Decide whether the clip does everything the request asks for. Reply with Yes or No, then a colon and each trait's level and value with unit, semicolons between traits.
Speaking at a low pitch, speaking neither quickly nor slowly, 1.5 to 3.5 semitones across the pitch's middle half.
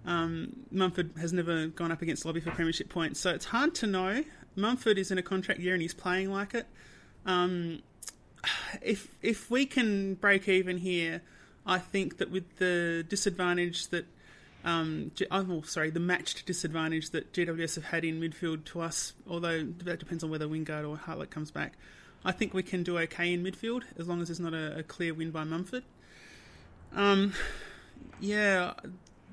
No: medium, 175 Hz; average, 180 wpm; narrow, 2.6 semitones